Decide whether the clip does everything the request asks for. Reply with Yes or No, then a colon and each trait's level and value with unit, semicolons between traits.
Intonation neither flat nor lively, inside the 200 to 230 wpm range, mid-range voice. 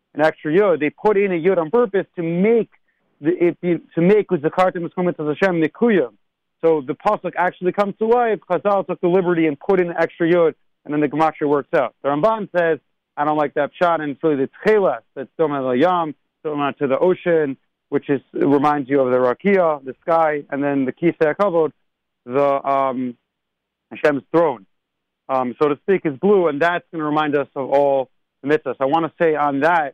Yes: average, 3.9 semitones; fast, 205 wpm; medium, 160 Hz